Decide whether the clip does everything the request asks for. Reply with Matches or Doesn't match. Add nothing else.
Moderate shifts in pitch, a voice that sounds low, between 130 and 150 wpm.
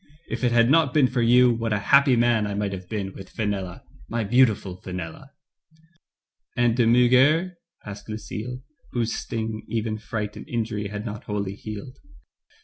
Doesn't match